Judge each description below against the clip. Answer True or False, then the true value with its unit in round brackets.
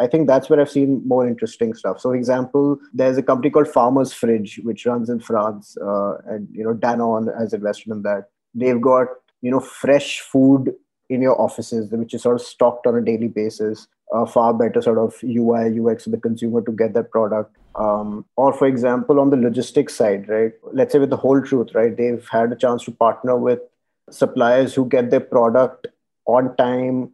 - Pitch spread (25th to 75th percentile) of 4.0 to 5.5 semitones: False (2.6 semitones)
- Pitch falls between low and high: False (120 Hz)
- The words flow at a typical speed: False (210 wpm)